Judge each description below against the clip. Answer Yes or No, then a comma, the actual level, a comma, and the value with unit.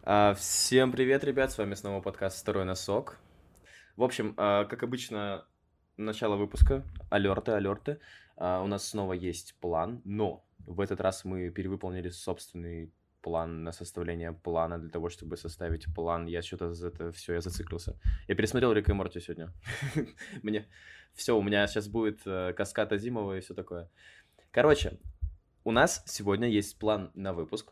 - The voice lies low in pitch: Yes, very low, 95 Hz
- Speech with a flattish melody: No, average, 3.4 semitones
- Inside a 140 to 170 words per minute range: Yes, fast, 160 wpm